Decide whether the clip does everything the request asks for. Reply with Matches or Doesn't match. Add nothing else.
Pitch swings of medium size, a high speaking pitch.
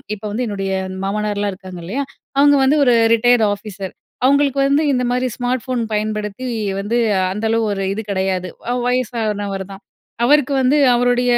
Matches